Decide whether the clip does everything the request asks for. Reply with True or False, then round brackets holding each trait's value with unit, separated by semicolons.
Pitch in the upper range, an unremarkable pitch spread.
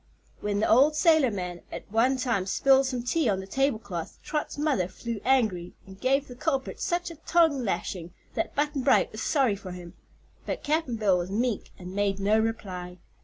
False (230 Hz; 6.1 semitones)